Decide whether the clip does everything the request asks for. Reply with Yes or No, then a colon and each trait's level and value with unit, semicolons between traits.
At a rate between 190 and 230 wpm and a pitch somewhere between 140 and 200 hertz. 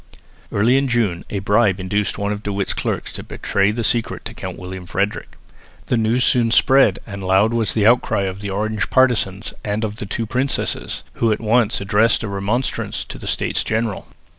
No: average, 195 wpm; low, 105 Hz